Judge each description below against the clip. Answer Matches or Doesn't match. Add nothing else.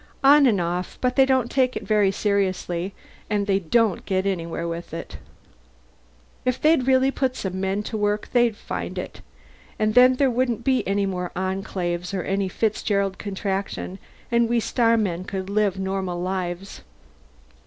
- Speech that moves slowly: Doesn't match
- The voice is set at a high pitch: Matches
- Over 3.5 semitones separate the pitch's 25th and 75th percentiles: Matches